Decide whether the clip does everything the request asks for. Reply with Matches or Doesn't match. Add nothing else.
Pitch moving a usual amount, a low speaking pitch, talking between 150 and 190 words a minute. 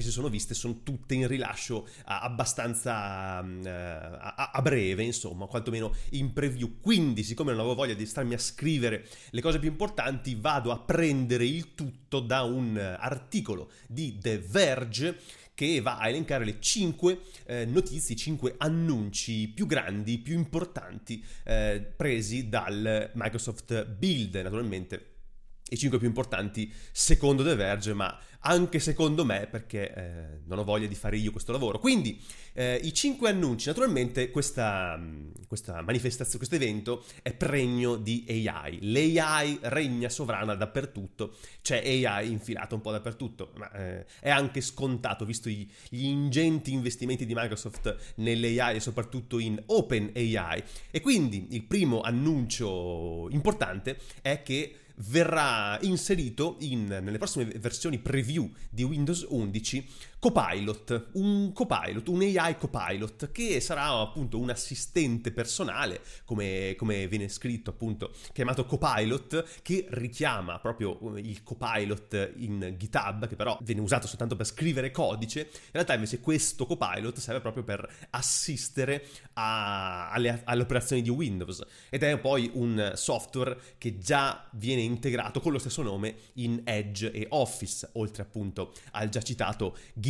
Doesn't match